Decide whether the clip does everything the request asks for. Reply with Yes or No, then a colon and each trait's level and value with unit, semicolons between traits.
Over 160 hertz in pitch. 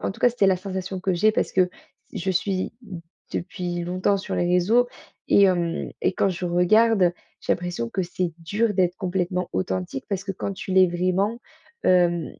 Yes: medium, 185 Hz